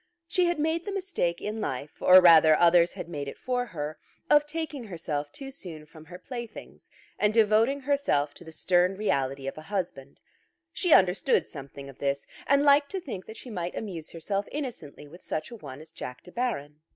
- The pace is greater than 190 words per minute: Yes, average, 200 wpm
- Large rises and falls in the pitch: Yes, wide, 8.5 semitones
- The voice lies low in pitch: No, medium, 180 Hz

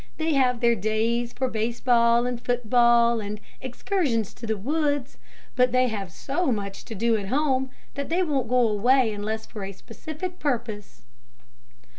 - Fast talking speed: No, average, 170 wpm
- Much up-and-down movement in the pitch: No, average, 3.2 semitones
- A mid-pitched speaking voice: No, high, 240 Hz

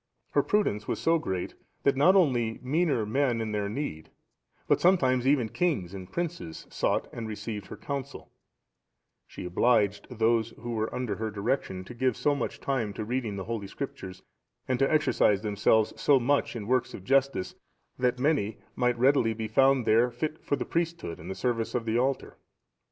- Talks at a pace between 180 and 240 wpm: Yes, average, 185 wpm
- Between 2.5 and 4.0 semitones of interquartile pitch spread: No, average, 4.4 semitones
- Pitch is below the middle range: Yes, low, 120 Hz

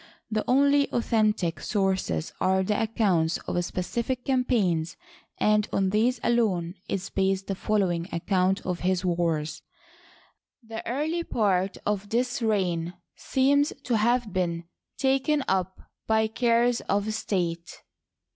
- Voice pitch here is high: Yes, high, 205 Hz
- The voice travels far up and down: No, average, 4.7 semitones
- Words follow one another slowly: Yes, slow, 125 wpm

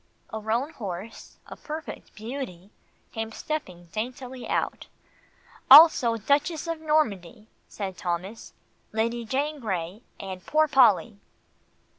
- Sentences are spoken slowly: Yes, slow, 110 wpm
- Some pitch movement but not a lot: No, wide, 6.1 semitones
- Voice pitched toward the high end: Yes, high, 230 Hz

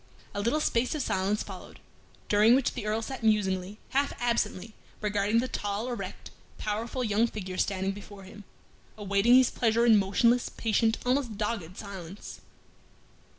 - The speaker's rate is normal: Yes, average, 150 wpm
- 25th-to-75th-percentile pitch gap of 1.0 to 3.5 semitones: Yes, average, 2.9 semitones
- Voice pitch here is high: Yes, high, 215 Hz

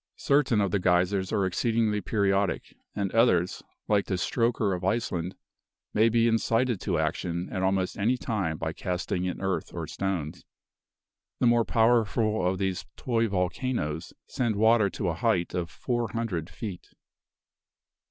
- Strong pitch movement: No, average, 4.1 semitones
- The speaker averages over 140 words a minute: Yes, average, 150 wpm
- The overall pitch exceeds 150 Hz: No, low, 100 Hz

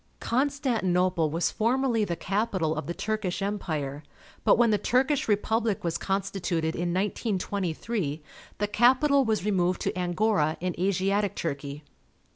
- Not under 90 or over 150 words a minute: Yes, slow, 135 wpm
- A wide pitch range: No, average, 4.3 semitones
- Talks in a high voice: Yes, high, 195 Hz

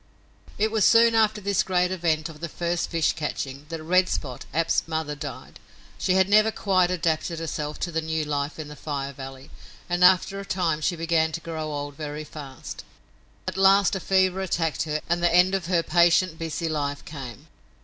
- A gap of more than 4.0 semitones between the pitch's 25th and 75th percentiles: No, average, 3.4 semitones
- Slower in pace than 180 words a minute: No, average, 195 wpm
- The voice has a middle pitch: Yes, medium, 165 Hz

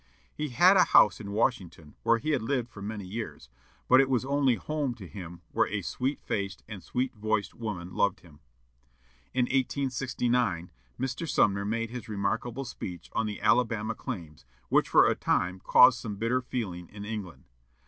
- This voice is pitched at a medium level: No, low, 110 Hz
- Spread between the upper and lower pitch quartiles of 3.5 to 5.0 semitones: Yes, average, 4.3 semitones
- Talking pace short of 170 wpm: No, average, 175 wpm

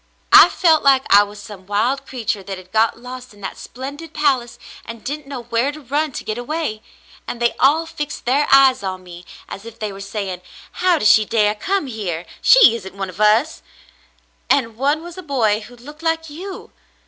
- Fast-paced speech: Yes, fast, 210 wpm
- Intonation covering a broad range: Yes, wide, 5.8 semitones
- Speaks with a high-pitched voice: Yes, high, 240 Hz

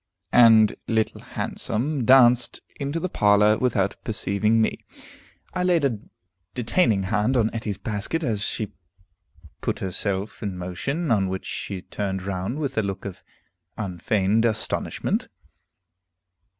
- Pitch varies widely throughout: No, average, 3.8 semitones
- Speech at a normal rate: No, slow, 125 wpm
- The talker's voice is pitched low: Yes, low, 110 Hz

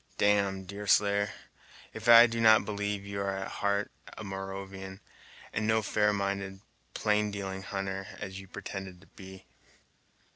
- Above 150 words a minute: No, average, 145 wpm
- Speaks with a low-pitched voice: Yes, low, 100 Hz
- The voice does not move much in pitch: Yes, narrow, 1.3 semitones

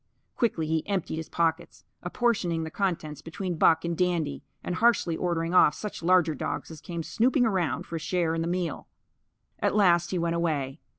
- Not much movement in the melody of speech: Yes, narrow, 2.2 semitones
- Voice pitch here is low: No, medium, 170 Hz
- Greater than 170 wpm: Yes, average, 185 wpm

